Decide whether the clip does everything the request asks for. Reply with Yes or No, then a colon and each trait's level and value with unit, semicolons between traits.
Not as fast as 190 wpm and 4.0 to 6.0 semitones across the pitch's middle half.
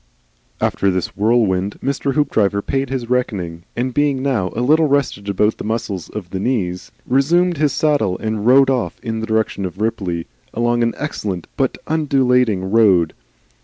Yes: average, 165 wpm; average, 5.3 semitones